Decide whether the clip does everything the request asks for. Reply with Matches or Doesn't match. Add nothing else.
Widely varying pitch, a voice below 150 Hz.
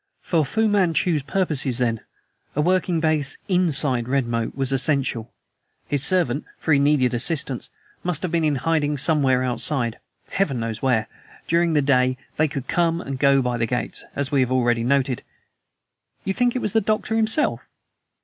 Doesn't match